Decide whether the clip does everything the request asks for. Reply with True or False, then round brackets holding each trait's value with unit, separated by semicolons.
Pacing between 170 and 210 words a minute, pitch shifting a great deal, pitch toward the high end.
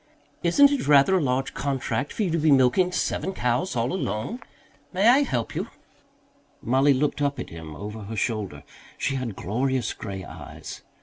False (175 wpm; 7.4 semitones; 135 Hz)